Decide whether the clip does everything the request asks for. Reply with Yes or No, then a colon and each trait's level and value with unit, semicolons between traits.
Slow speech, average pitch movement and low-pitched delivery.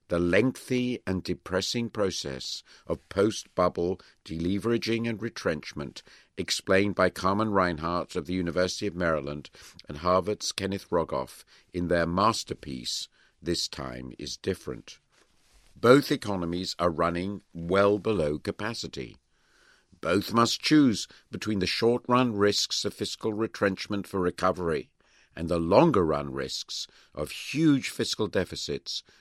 Yes: slow, 125 wpm; average, 4.2 semitones; very low, 95 Hz